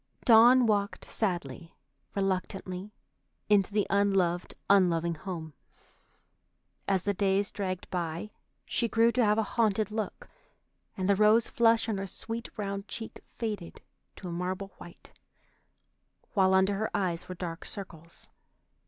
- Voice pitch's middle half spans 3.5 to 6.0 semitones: No, average, 2.8 semitones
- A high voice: Yes, high, 195 Hz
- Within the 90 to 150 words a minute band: Yes, slow, 135 wpm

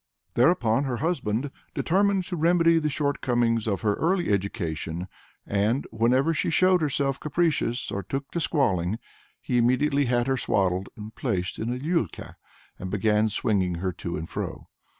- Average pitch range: No, wide, 6.6 semitones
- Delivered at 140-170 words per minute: Yes, average, 160 wpm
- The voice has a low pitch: Yes, low, 120 Hz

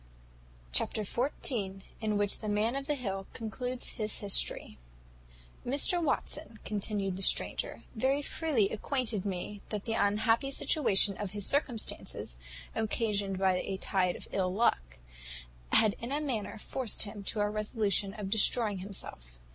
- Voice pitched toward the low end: No, high, 210 Hz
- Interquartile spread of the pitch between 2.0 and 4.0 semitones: Yes, average, 3.4 semitones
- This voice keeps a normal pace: Yes, average, 145 wpm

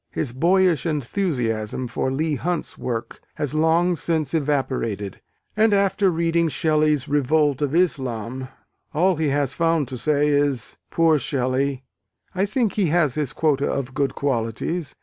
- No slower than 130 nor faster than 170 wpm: Yes, average, 145 wpm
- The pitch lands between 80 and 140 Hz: No, medium, 150 Hz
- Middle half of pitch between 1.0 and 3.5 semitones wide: No, average, 4.0 semitones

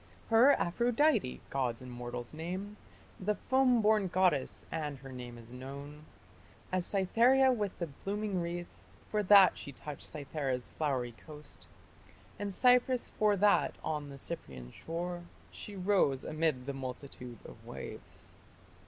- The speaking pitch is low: No, medium, 165 Hz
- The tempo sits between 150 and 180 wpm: No, slow, 135 wpm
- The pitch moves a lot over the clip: Yes, wide, 7.3 semitones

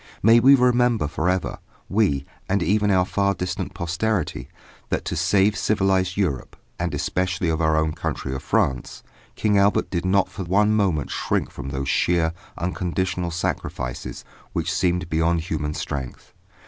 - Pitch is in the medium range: No, very low, 90 Hz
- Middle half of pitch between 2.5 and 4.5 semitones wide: Yes, average, 3.7 semitones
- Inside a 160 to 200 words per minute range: No, average, 150 wpm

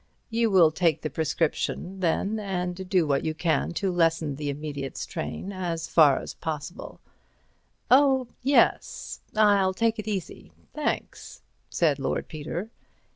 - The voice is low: No, medium, 175 Hz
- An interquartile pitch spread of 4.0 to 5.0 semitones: Yes, average, 4.3 semitones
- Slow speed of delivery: Yes, slow, 130 wpm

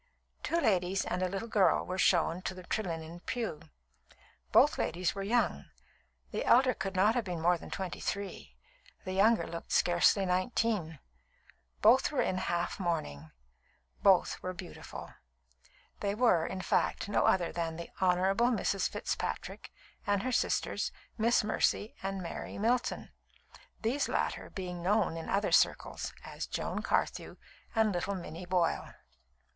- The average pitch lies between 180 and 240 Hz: Yes, high, 190 Hz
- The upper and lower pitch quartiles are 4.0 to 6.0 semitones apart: No, average, 3.6 semitones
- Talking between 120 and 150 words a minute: Yes, average, 145 wpm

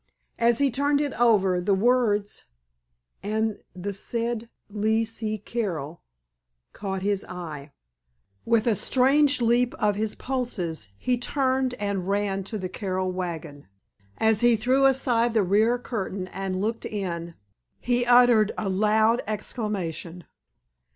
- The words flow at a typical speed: No, slow, 130 wpm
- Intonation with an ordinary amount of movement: Yes, average, 4.0 semitones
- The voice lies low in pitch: No, high, 215 Hz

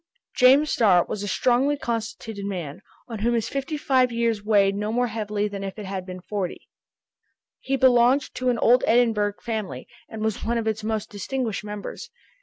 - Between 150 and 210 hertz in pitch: No, high, 220 Hz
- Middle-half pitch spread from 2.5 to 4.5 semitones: Yes, average, 3.2 semitones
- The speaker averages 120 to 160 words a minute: No, average, 185 wpm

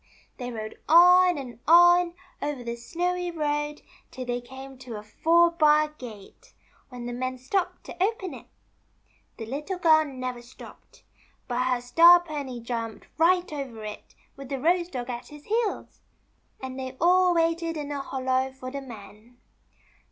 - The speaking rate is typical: Yes, average, 160 wpm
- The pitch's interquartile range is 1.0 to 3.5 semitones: No, wide, 5.4 semitones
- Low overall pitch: No, very high, 275 Hz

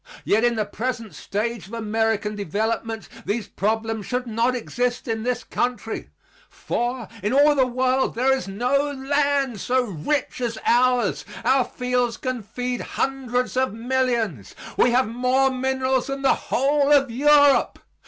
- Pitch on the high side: Yes, high, 245 Hz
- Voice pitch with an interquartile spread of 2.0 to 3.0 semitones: Yes, average, 2.7 semitones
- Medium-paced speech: Yes, average, 150 wpm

